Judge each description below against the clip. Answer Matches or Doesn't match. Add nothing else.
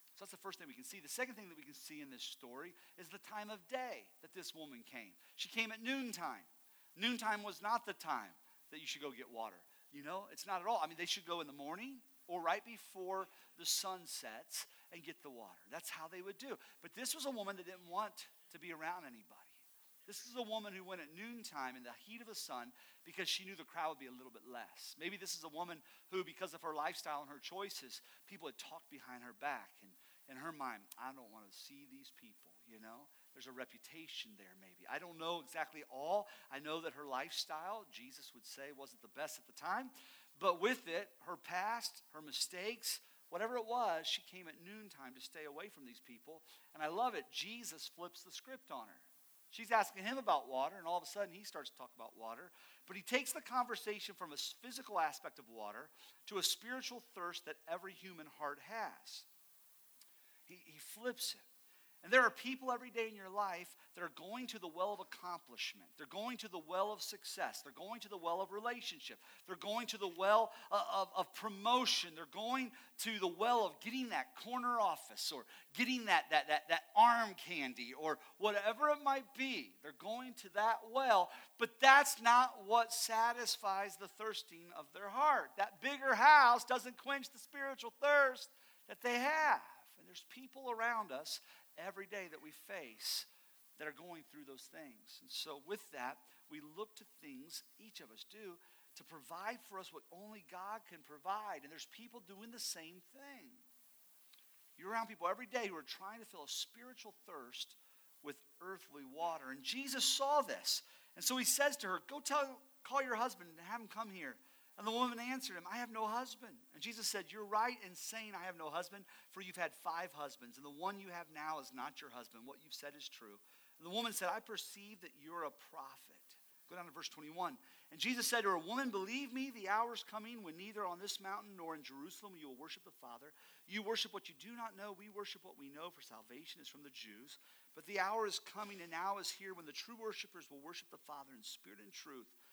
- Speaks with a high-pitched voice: Matches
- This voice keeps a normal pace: Doesn't match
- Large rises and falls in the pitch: Matches